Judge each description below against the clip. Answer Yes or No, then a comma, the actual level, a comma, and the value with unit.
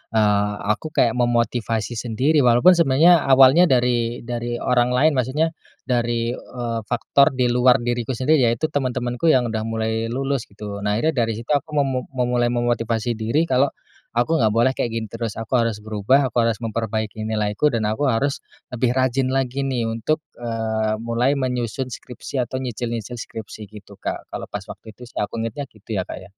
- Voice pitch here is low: Yes, low, 120 Hz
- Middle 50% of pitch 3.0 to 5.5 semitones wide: No, narrow, 2.6 semitones